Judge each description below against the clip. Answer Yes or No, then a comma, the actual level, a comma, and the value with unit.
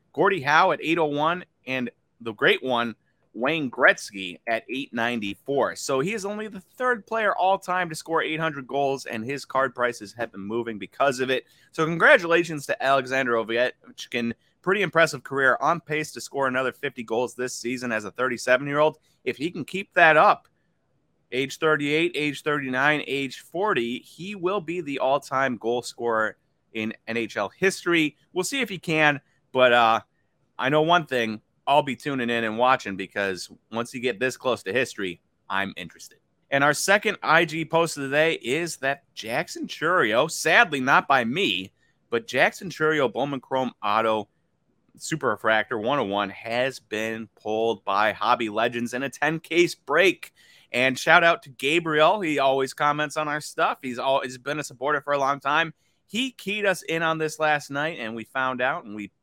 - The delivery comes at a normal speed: Yes, average, 175 wpm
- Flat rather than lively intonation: No, average, 4.9 semitones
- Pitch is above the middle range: No, low, 135 Hz